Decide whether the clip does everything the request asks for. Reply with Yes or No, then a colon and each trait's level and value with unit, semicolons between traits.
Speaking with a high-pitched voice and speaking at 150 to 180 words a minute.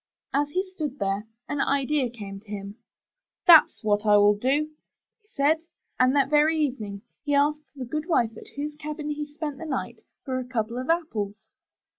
No: very high, 280 Hz; average, 190 wpm